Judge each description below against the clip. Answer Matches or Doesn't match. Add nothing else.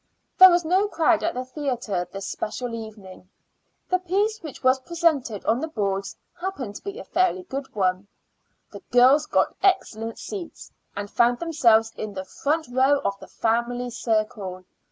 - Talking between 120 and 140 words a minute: Doesn't match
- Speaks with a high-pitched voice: Matches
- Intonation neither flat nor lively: Doesn't match